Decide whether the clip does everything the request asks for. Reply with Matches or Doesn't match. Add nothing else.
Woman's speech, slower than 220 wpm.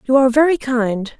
Matches